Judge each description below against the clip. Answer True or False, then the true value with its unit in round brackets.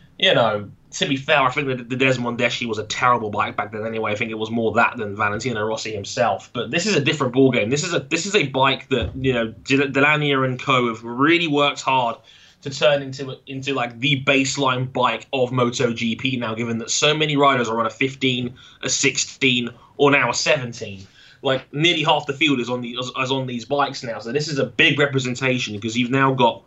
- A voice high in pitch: False (130 Hz)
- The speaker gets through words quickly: True (225 wpm)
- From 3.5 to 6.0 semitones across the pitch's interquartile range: False (2.8 semitones)